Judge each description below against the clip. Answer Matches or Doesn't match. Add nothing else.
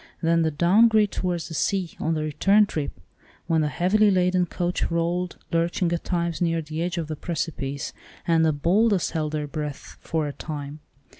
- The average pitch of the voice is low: Doesn't match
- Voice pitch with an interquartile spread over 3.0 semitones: Doesn't match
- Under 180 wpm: Doesn't match